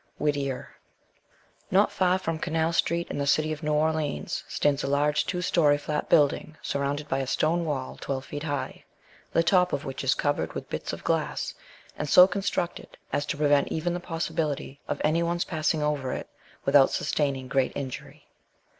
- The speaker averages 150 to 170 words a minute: No, average, 180 wpm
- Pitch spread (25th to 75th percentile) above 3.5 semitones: No, average, 2.8 semitones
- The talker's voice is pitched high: No, medium, 150 Hz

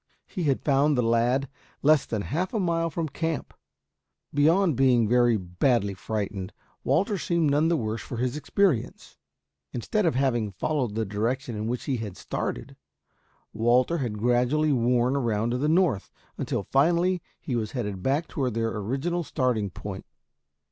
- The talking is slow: No, average, 160 wpm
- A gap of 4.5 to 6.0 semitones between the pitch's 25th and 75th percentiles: Yes, wide, 5.4 semitones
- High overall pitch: No, low, 125 Hz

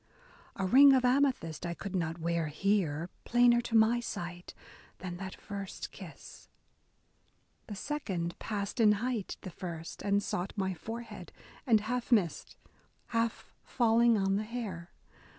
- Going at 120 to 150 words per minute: Yes, average, 140 wpm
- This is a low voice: No, high, 200 Hz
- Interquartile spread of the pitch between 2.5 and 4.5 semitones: No, average, 5.0 semitones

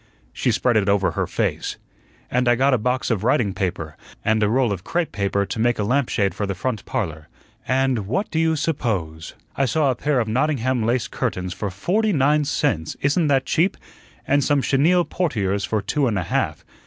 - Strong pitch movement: Yes, wide, 5.8 semitones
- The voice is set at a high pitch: No, low, 120 Hz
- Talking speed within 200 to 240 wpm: Yes, fast, 205 wpm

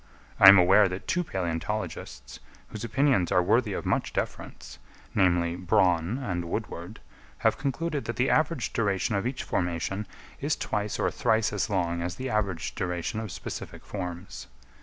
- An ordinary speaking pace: Yes, average, 160 wpm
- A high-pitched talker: No, very low, 95 Hz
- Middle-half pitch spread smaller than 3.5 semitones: No, average, 4.4 semitones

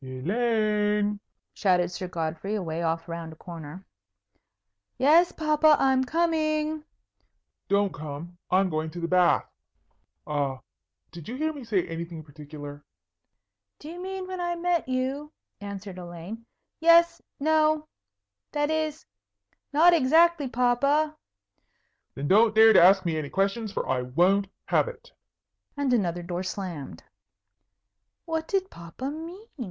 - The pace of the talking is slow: Yes, slow, 130 wpm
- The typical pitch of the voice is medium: No, high, 210 Hz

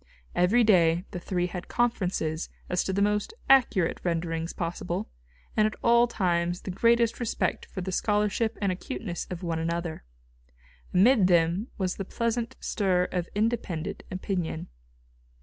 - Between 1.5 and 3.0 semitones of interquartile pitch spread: No, average, 4.0 semitones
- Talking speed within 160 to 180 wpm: No, average, 145 wpm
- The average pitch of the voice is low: No, medium, 185 Hz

